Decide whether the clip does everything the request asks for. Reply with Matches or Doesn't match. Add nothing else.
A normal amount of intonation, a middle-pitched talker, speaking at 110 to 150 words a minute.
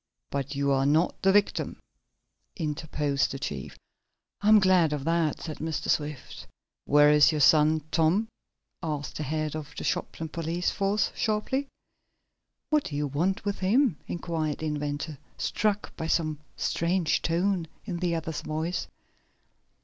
Matches